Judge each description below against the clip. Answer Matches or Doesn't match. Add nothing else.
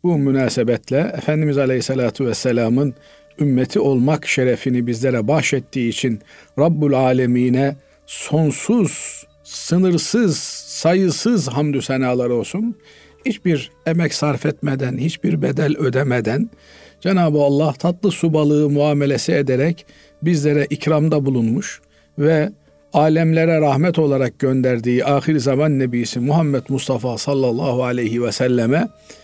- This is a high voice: Doesn't match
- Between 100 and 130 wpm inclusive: Matches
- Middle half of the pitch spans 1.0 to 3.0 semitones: Doesn't match